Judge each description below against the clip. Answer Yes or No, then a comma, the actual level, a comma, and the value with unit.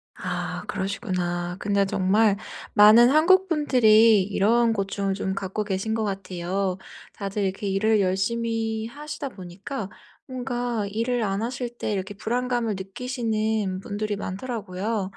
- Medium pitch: No, high, 210 Hz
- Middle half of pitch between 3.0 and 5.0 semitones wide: Yes, average, 3.3 semitones